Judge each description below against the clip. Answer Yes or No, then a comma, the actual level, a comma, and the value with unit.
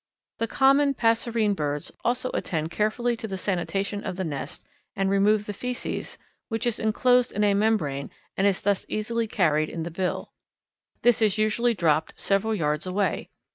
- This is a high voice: Yes, high, 205 Hz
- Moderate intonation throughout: Yes, average, 3.9 semitones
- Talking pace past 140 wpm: Yes, average, 170 wpm